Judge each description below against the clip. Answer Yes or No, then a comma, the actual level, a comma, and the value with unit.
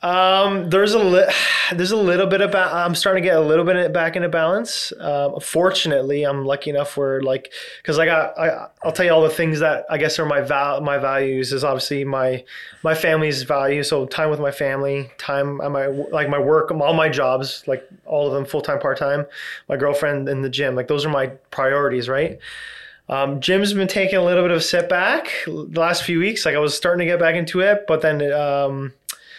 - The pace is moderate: No, fast, 225 wpm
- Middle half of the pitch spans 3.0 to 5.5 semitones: Yes, average, 3.9 semitones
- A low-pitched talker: No, medium, 150 Hz